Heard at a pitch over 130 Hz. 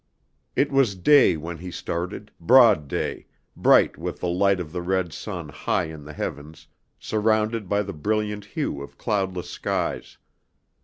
No: very low, 95 Hz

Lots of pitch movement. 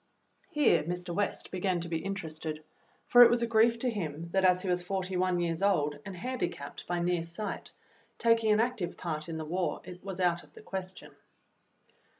No: average, 3.3 semitones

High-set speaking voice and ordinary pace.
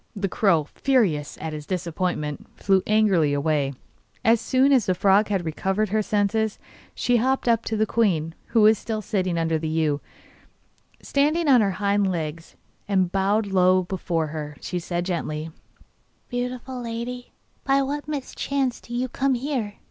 Yes: high, 200 Hz; average, 160 wpm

